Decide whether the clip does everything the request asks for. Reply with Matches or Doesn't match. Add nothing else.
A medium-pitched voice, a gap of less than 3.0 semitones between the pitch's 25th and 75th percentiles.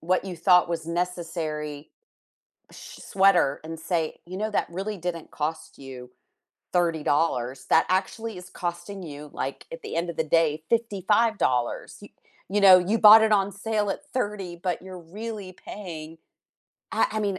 Doesn't match